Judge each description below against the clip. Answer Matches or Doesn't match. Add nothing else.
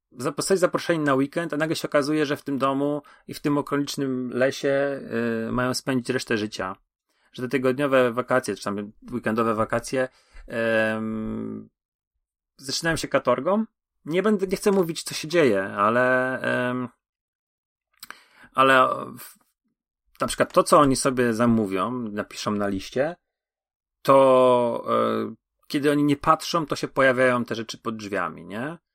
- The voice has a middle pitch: Doesn't match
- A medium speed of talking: Matches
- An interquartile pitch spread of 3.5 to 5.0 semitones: Matches